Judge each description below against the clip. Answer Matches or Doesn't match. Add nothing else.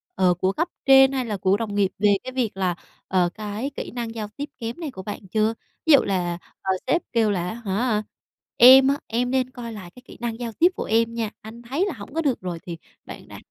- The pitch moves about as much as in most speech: Matches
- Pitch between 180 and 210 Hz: Doesn't match